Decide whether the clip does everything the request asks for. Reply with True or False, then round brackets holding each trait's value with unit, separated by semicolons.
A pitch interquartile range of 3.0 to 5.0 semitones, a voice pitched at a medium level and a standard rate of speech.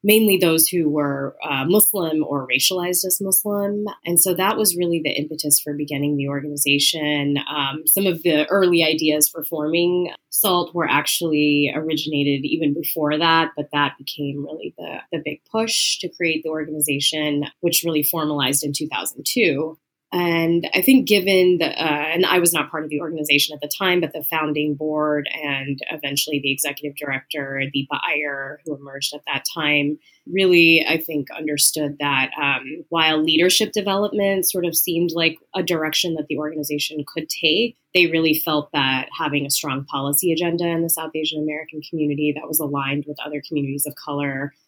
False (2.6 semitones; 155 Hz; 175 wpm)